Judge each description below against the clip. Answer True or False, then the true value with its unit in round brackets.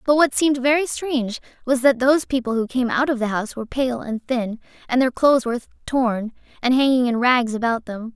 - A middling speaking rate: False (220 wpm)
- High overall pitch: True (250 Hz)